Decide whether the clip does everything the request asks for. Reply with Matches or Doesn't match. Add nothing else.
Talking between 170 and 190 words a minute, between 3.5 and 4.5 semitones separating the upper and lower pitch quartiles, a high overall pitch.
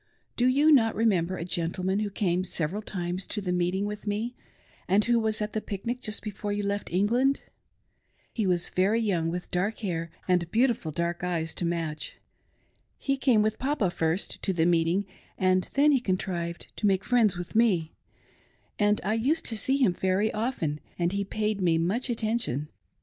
Matches